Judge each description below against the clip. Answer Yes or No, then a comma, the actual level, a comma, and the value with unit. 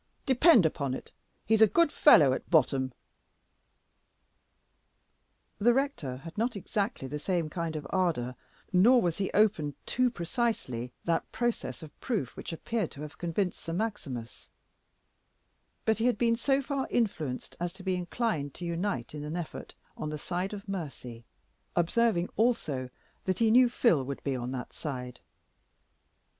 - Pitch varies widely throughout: Yes, wide, 7.5 semitones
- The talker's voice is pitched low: No, medium, 175 Hz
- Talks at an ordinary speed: Yes, average, 155 wpm